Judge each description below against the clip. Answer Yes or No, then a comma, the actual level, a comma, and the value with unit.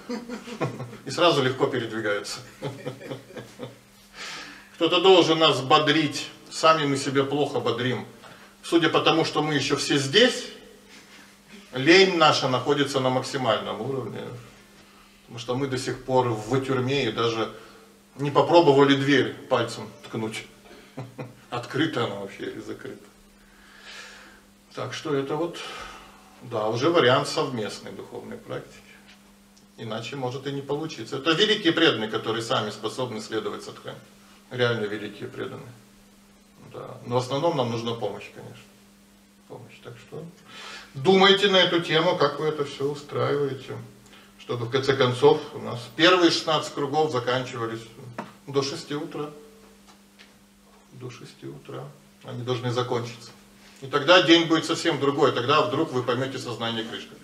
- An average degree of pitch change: Yes, average, 5.0 semitones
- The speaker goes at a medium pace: Yes, average, 130 wpm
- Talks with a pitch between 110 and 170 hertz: Yes, low, 135 Hz